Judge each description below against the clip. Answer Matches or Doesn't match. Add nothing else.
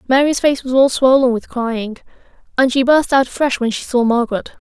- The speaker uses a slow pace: Doesn't match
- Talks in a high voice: Matches